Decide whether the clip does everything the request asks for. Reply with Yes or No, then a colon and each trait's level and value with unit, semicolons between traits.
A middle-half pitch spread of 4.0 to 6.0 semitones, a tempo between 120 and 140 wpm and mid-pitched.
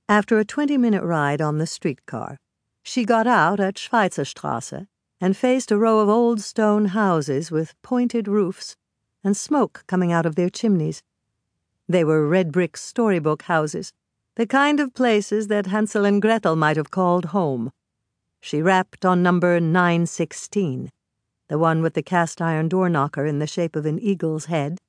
No: average, 5.2 semitones; average, 165 wpm; medium, 180 Hz